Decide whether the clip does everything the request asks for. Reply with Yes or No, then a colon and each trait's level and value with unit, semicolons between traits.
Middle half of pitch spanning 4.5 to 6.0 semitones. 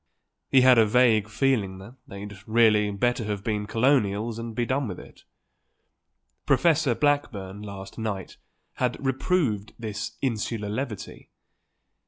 No: average, 3.6 semitones